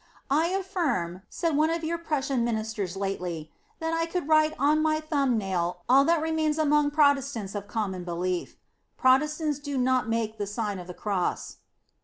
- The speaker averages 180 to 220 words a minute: Yes, average, 185 wpm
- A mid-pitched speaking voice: No, very high, 270 Hz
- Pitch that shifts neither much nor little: No, wide, 7.3 semitones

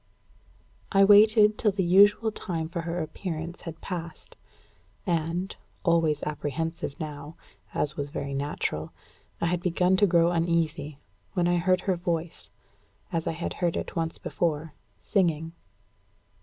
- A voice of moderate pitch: Yes, medium, 170 Hz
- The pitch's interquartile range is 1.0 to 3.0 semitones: Yes, narrow, 2.4 semitones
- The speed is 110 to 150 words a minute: Yes, average, 140 wpm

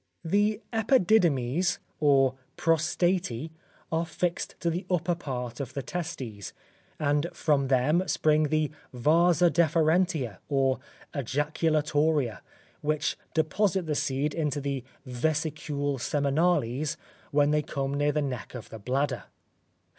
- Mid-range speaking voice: Yes, medium, 150 Hz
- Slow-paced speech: Yes, slow, 115 wpm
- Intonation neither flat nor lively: Yes, average, 3.5 semitones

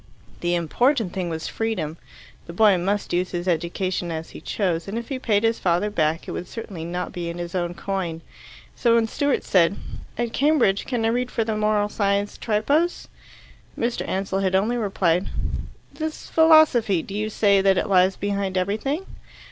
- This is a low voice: No, high, 200 Hz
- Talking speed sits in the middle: Yes, average, 180 wpm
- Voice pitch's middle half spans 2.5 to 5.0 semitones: Yes, average, 4.3 semitones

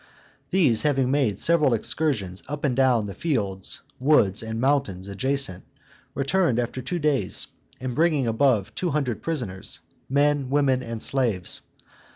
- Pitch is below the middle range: Yes, low, 130 Hz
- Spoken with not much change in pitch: No, average, 4.5 semitones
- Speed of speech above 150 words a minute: No, slow, 135 wpm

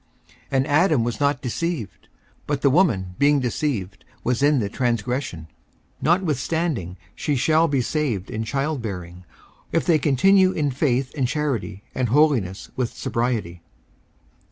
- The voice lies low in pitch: Yes, low, 130 Hz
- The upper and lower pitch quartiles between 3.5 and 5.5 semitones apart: Yes, average, 5.2 semitones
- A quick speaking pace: No, average, 140 wpm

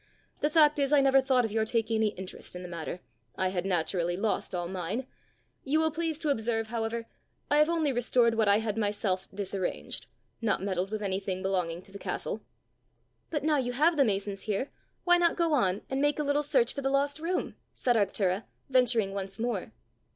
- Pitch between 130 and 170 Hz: No, high, 225 Hz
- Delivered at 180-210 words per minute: Yes, average, 200 wpm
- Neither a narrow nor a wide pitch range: No, wide, 6.5 semitones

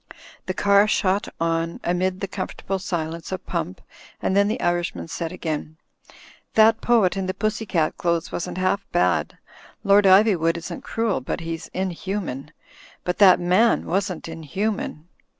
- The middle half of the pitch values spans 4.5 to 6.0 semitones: No, average, 3.1 semitones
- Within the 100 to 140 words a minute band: No, average, 150 wpm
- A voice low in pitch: No, medium, 185 Hz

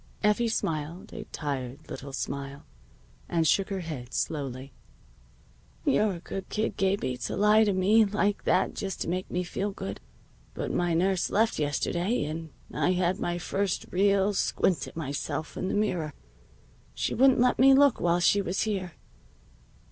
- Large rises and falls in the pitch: No, average, 4.7 semitones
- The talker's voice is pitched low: No, medium, 185 Hz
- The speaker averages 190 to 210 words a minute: No, average, 155 wpm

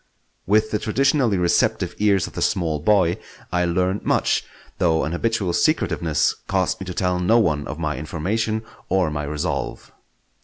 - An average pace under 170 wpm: Yes, average, 160 wpm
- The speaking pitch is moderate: No, very low, 90 Hz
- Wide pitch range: No, average, 4.5 semitones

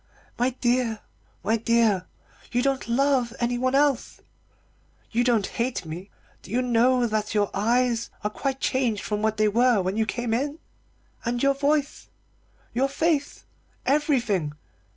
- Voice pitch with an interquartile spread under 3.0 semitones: No, average, 3.3 semitones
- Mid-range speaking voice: No, high, 240 Hz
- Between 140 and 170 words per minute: Yes, average, 150 wpm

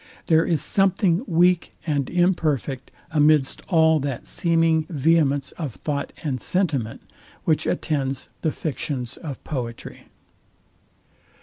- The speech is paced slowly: Yes, slow, 110 wpm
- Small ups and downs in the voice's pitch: No, average, 3.4 semitones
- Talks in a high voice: No, medium, 155 Hz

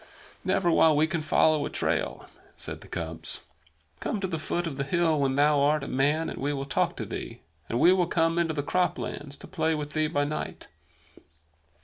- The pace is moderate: No, fast, 210 wpm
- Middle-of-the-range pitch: Yes, medium, 155 Hz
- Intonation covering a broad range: No, narrow, 2.5 semitones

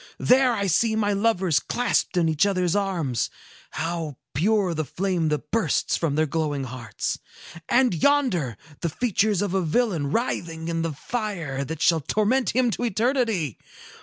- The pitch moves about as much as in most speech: No, wide, 5.9 semitones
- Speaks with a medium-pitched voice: Yes, medium, 180 Hz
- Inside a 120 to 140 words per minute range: No, average, 160 wpm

